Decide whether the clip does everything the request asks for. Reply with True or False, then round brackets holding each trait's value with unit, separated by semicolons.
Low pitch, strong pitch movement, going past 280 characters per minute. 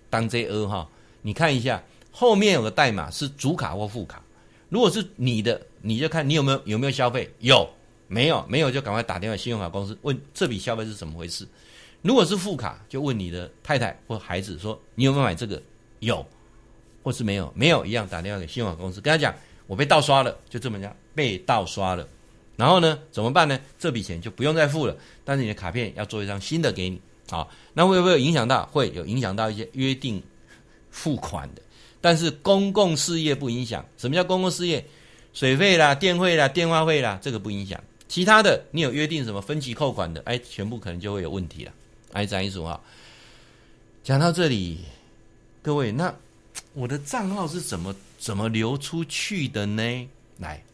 True (120 Hz; 6.9 semitones; 300 characters per minute)